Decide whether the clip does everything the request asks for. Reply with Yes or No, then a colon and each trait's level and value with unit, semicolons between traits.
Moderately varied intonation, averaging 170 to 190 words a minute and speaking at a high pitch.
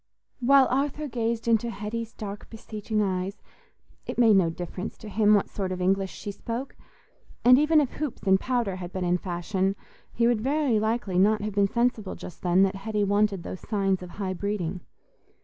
Yes: average, 3.5 semitones; average, 185 wpm; high, 210 Hz